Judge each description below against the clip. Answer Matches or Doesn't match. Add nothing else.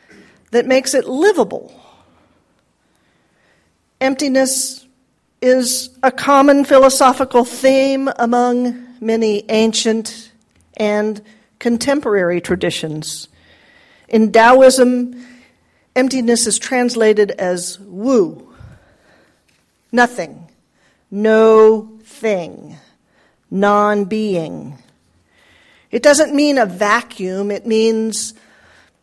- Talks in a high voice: Matches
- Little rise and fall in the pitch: Doesn't match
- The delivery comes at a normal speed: Doesn't match